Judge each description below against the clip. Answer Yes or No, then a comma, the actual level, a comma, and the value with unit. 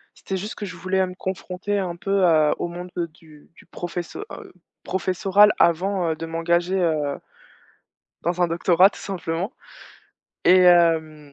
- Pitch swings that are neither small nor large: No, narrow, 2.3 semitones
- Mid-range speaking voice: Yes, medium, 175 Hz